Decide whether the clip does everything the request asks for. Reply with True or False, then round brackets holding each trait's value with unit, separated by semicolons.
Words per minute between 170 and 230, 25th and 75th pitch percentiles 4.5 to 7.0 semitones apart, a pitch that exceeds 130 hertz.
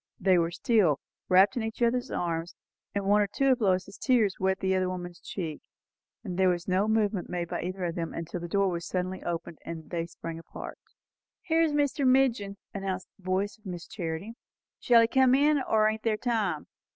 False (200 wpm; 4.1 semitones; 190 Hz)